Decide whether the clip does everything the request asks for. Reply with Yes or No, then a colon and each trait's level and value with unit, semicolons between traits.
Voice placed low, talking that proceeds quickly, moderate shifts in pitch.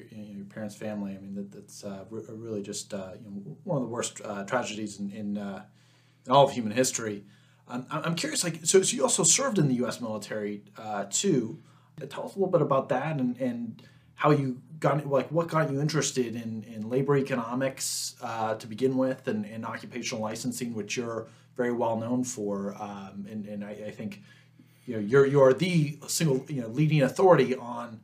Yes: low, 125 Hz; fast, 210 wpm; average, 4.5 semitones